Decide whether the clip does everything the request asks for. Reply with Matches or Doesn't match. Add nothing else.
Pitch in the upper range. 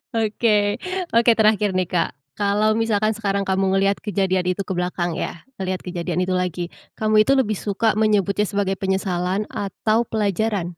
Matches